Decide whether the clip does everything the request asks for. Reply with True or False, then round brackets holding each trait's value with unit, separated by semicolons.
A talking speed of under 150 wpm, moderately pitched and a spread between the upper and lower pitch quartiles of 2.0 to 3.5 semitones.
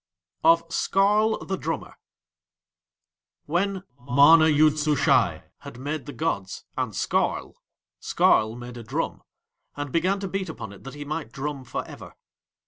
False (140 wpm; 150 Hz; 4.5 semitones)